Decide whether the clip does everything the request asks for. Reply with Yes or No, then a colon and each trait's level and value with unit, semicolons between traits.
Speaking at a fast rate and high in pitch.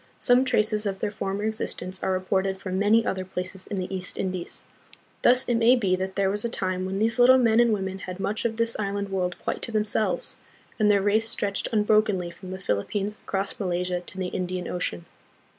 Yes: fast, 210 wpm; high, 195 Hz